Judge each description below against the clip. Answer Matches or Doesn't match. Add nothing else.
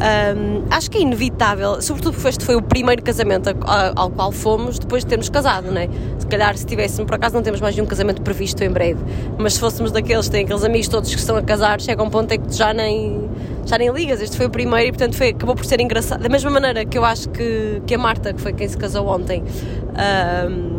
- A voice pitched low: Matches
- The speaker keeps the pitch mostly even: Matches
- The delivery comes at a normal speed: Doesn't match